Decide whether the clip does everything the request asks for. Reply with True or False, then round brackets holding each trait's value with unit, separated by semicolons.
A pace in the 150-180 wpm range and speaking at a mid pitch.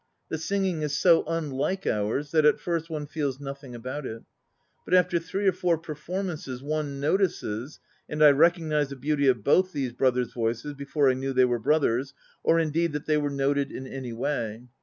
False (190 wpm; 145 Hz)